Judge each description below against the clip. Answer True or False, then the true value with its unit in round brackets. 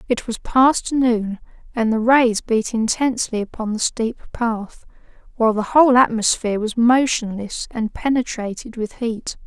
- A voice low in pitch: False (230 Hz)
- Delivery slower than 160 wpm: True (145 wpm)